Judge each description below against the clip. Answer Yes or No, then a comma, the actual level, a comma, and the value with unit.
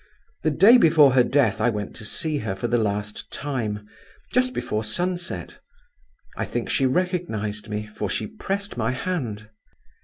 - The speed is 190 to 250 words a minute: No, average, 160 wpm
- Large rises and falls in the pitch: Yes, wide, 8.5 semitones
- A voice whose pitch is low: Yes, low, 125 Hz